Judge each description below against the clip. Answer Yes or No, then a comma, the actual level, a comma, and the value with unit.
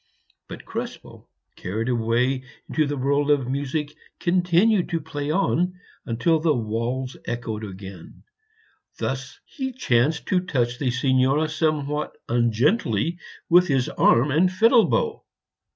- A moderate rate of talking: No, slow, 130 wpm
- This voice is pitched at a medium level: Yes, medium, 145 Hz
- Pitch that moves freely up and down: Yes, wide, 5.9 semitones